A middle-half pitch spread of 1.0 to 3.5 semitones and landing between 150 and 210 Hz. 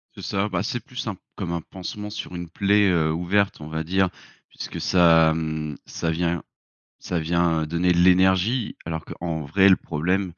No: average, 2.8 semitones; very low, 85 Hz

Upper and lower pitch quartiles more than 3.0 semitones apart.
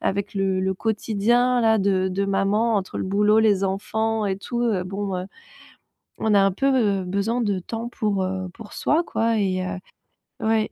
No: narrow, 2.6 semitones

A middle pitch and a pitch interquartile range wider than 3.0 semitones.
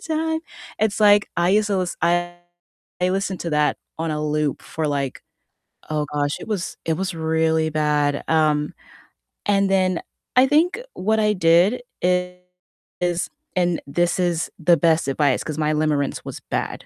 Yes: medium, 170 Hz; average, 3.7 semitones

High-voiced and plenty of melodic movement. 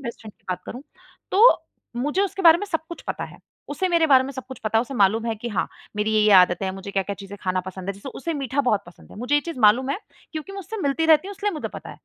Yes: very high, 260 Hz; wide, 7.7 semitones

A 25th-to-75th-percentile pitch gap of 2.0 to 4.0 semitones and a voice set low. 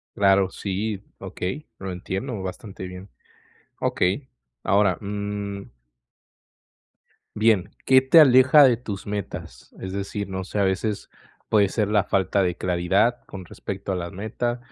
Yes: narrow, 2.5 semitones; low, 100 Hz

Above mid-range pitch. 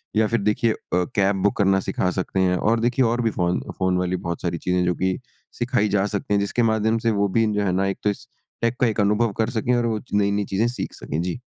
No: low, 105 Hz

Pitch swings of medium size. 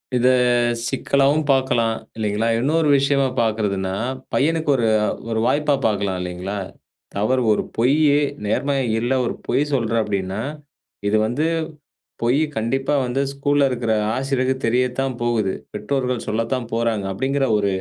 Yes: average, 4.0 semitones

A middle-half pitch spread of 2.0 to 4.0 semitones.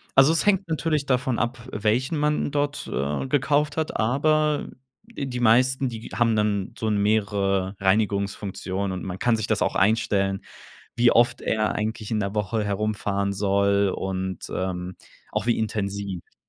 No: average, 4.6 semitones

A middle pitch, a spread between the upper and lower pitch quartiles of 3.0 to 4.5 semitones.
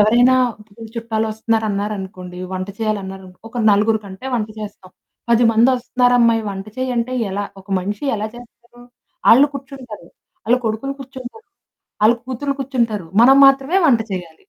No: high, 225 Hz; average, 3.6 semitones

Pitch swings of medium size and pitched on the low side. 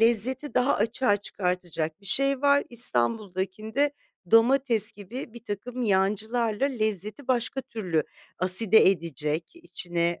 No: average, 4.9 semitones; high, 220 Hz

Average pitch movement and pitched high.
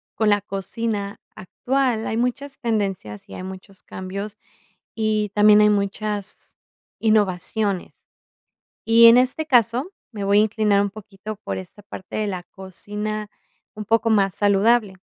No: narrow, 2.2 semitones; high, 210 Hz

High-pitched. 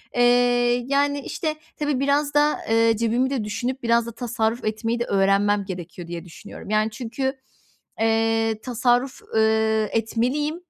Yes: high, 230 Hz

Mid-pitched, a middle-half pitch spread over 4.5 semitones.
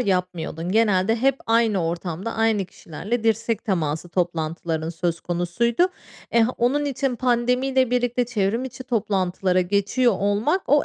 No: high, 215 Hz; average, 5.3 semitones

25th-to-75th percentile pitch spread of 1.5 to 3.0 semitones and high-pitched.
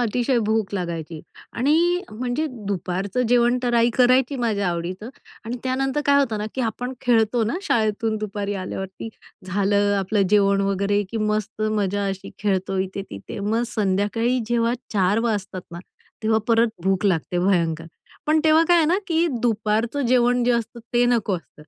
No: average, 3.6 semitones; high, 215 Hz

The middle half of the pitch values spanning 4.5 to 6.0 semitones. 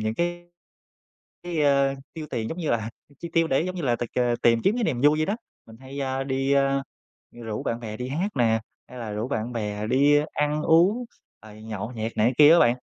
Yes: average, 5.1 semitones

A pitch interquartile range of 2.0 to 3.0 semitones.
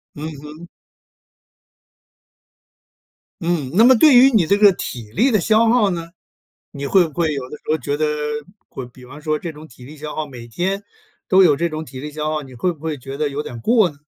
No: average, 4.7 semitones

